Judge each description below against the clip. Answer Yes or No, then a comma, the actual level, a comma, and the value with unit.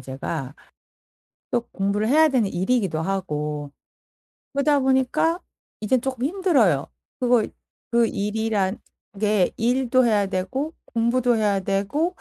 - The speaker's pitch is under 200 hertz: No, high, 225 Hz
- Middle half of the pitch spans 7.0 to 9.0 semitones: No, average, 5.1 semitones